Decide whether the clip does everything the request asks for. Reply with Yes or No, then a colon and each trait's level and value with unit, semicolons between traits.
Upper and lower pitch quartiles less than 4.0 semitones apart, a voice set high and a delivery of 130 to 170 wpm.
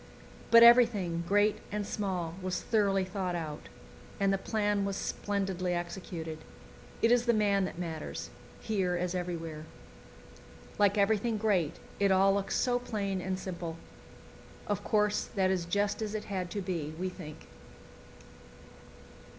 Yes: average, 2.8 semitones; high, 195 Hz; average, 140 wpm